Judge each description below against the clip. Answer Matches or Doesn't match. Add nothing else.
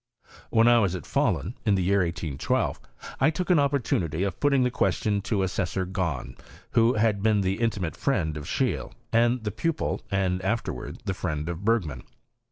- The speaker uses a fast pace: Doesn't match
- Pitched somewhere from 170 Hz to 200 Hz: Doesn't match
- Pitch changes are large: Doesn't match